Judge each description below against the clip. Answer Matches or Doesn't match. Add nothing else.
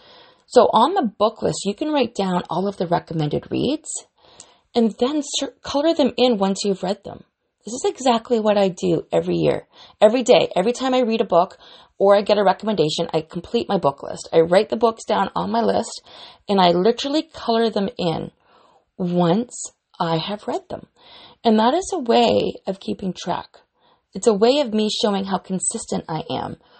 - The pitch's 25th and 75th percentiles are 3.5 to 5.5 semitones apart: Matches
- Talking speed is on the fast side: Doesn't match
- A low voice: Doesn't match